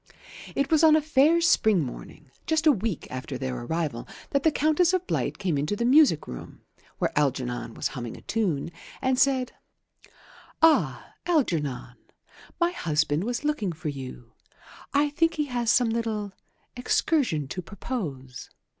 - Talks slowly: No, average, 155 wpm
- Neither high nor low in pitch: No, high, 220 Hz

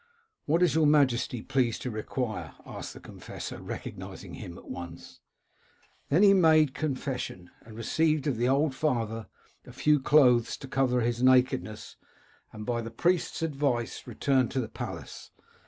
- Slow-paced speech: No, average, 165 wpm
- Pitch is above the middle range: No, low, 130 Hz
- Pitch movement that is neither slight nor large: Yes, average, 4.5 semitones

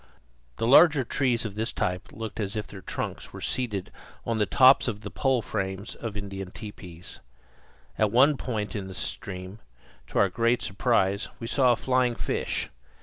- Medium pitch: No, low, 110 Hz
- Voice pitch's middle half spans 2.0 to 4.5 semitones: Yes, average, 4.0 semitones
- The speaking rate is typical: Yes, average, 175 wpm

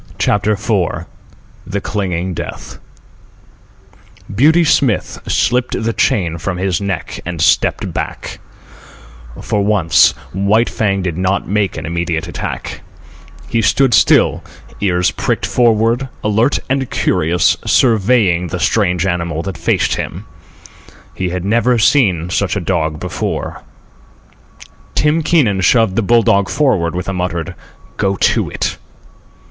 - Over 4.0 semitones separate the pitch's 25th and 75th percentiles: Yes, average, 4.5 semitones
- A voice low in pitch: Yes, low, 100 Hz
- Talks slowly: Yes, slow, 130 wpm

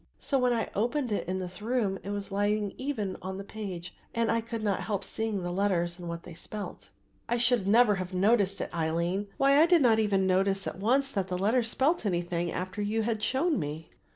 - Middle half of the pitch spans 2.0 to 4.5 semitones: Yes, average, 3.8 semitones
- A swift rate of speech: Yes, fast, 220 wpm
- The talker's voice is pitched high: Yes, high, 205 Hz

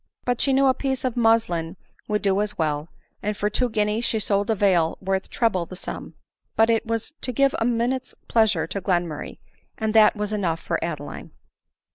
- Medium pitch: No, high, 210 Hz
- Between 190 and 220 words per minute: Yes, average, 195 wpm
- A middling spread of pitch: Yes, average, 4.0 semitones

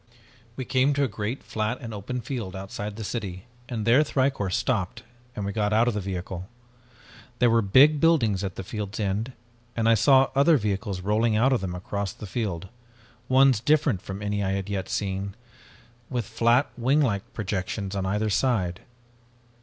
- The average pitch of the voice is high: No, low, 105 Hz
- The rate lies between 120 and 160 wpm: No, average, 175 wpm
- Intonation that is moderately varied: Yes, average, 4.3 semitones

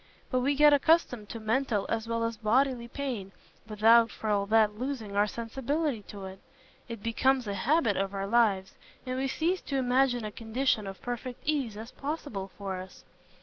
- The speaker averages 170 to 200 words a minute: Yes, average, 185 wpm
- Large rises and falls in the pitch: No, average, 4.2 semitones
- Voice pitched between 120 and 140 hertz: No, high, 230 Hz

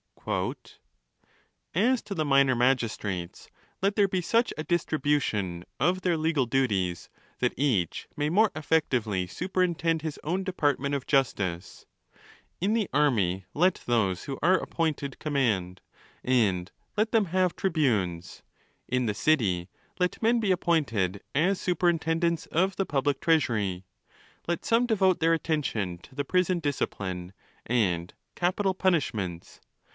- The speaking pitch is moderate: Yes, medium, 145 Hz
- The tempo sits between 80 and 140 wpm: Yes, slow, 135 wpm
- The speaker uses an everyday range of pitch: No, wide, 8.9 semitones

